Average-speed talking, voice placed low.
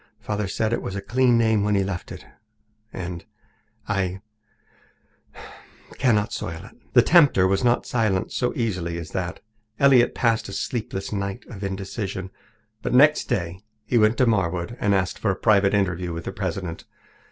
Yes: average, 165 wpm; low, 100 Hz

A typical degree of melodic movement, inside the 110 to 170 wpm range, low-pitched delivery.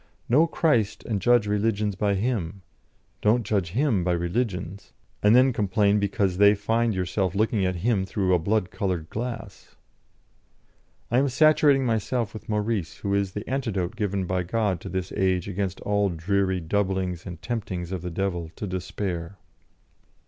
Yes: average, 3.3 semitones; average, 160 wpm; low, 100 Hz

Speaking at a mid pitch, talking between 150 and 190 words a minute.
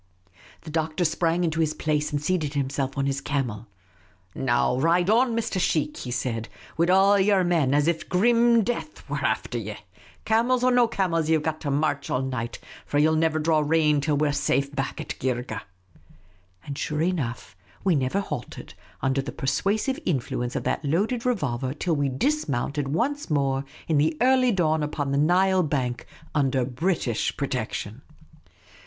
Yes: medium, 150 Hz; average, 180 wpm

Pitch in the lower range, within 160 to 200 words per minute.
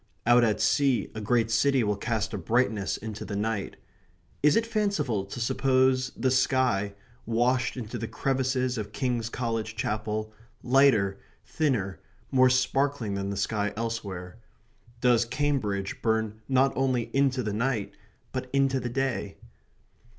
No: low, 120 Hz; average, 145 wpm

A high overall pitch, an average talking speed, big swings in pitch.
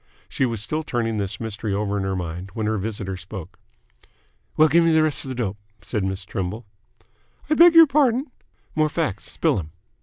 No: low, 110 Hz; average, 190 wpm; wide, 8.2 semitones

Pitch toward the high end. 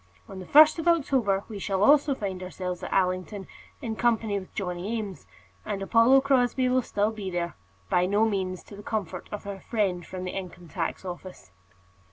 Yes: high, 200 Hz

